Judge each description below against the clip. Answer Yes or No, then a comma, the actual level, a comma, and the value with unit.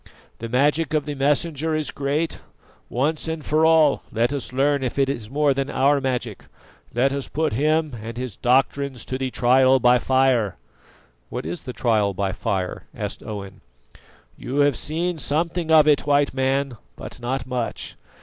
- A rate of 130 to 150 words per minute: No, average, 170 wpm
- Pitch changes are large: No, average, 3.2 semitones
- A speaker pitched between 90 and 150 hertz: Yes, low, 135 Hz